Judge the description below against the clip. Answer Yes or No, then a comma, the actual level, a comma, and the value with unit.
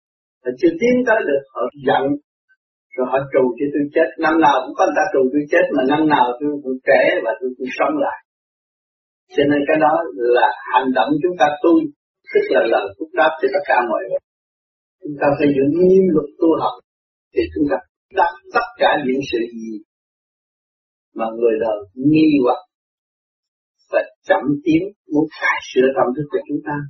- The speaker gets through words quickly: No, average, 190 wpm